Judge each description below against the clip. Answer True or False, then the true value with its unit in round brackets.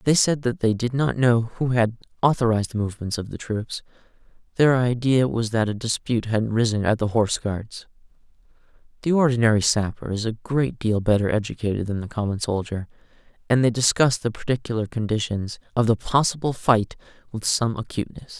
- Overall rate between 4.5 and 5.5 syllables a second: False (5.7 syllables/s)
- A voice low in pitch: True (115 Hz)